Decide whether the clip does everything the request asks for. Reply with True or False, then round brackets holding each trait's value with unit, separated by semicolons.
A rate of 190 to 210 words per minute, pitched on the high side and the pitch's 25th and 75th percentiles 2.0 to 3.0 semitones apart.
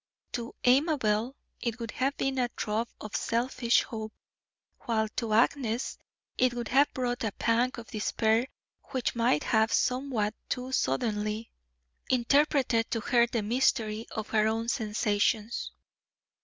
False (135 wpm; 230 Hz; 2.4 semitones)